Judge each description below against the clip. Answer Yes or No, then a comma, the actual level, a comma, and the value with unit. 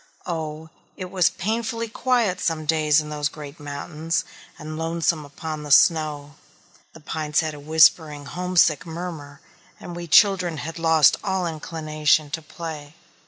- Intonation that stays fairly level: Yes, narrow, 2.3 semitones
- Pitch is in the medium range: Yes, medium, 160 Hz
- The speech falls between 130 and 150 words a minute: Yes, average, 145 wpm